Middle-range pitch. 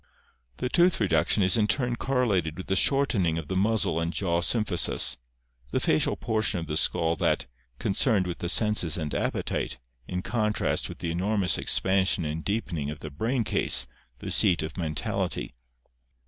No: very low, 95 Hz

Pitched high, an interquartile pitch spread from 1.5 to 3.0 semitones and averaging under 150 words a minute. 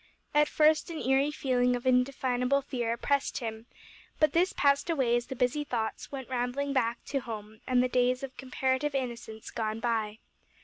No: very high, 255 Hz; narrow, 2.6 semitones; average, 175 wpm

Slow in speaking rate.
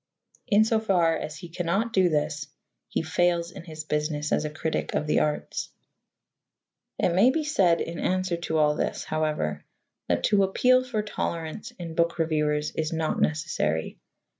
No: average, 165 wpm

